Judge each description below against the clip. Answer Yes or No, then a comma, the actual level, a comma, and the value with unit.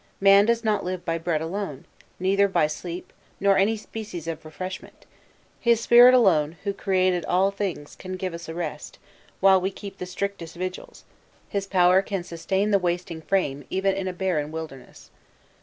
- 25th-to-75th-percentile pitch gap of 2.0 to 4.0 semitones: Yes, average, 2.9 semitones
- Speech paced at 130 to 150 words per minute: No, average, 175 wpm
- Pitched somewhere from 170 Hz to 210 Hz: Yes, medium, 185 Hz